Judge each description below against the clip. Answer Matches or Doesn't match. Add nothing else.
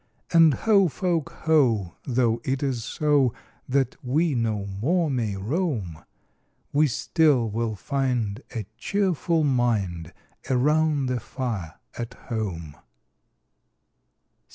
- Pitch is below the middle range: Matches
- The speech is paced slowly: Matches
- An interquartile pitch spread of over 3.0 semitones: Matches